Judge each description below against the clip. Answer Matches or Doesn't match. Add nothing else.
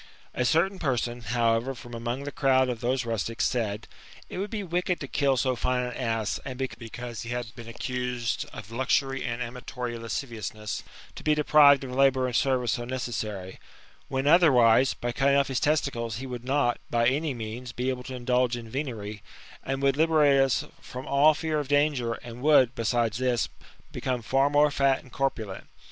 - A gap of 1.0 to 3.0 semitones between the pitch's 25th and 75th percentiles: Matches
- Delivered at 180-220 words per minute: Matches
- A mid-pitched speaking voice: Doesn't match